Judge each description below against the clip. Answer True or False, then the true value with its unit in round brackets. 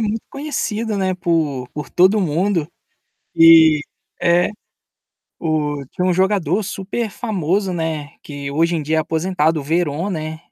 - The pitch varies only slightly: False (3.6 semitones)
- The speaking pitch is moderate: True (170 Hz)